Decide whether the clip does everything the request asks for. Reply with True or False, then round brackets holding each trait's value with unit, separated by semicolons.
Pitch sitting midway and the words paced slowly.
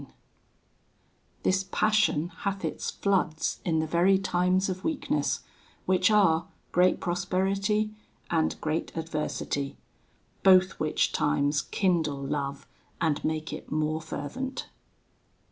True (175 Hz; 110 wpm)